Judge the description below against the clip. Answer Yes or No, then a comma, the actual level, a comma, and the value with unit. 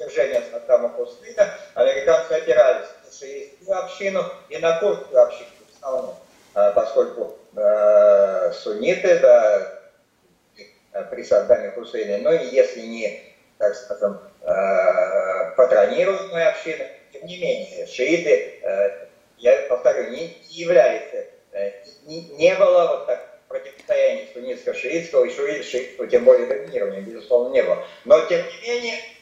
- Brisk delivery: No, average, 125 wpm